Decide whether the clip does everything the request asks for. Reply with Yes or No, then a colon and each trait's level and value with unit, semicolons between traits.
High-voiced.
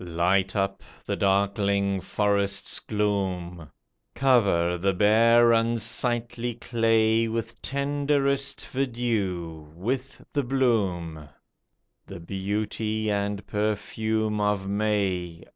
No: low, 105 Hz